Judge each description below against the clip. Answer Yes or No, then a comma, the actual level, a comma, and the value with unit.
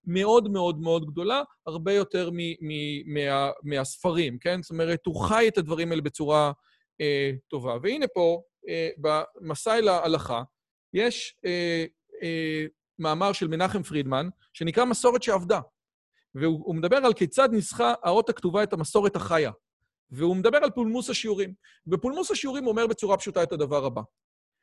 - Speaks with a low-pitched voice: No, medium, 175 Hz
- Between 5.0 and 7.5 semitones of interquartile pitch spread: Yes, wide, 5.6 semitones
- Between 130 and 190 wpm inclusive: Yes, fast, 150 wpm